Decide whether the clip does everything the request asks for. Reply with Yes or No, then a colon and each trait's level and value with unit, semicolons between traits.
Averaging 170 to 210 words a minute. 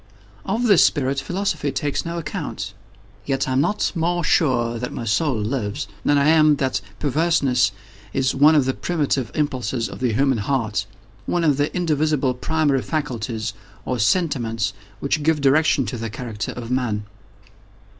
No: average, 155 wpm